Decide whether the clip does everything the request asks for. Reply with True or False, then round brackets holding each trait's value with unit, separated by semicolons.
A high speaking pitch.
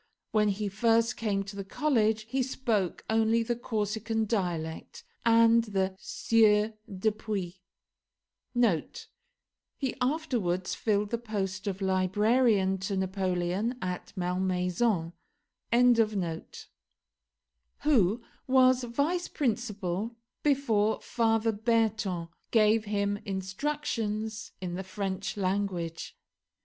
True (215 Hz)